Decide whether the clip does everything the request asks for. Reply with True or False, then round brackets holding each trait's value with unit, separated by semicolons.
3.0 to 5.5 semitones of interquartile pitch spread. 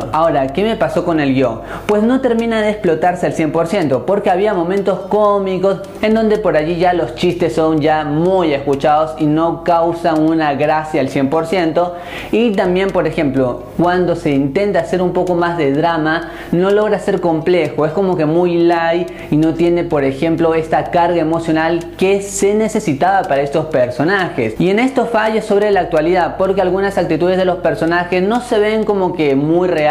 True (3.5 semitones)